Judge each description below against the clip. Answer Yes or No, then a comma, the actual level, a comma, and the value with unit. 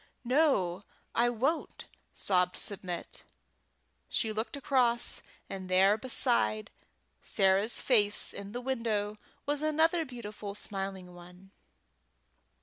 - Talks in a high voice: Yes, high, 210 Hz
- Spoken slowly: Yes, slow, 100 wpm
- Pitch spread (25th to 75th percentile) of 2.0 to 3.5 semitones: No, average, 4.6 semitones